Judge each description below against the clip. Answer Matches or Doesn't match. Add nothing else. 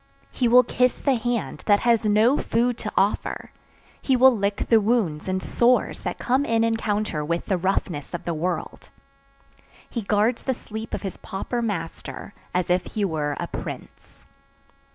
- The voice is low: Doesn't match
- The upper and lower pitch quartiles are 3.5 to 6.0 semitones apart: Matches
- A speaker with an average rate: Matches